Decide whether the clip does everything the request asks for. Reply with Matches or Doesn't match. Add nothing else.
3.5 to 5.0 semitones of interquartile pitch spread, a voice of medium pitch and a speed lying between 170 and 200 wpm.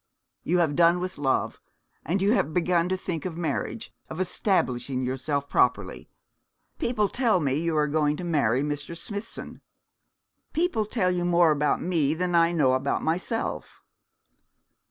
Doesn't match